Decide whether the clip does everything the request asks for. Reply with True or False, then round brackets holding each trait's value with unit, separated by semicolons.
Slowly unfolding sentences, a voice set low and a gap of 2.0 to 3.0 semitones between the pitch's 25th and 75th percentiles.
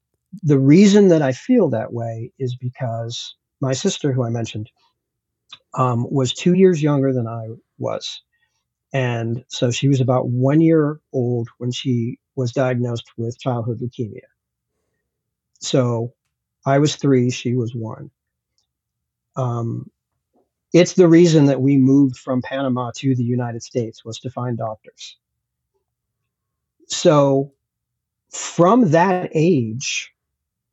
False (125 wpm; 130 Hz; 3.4 semitones)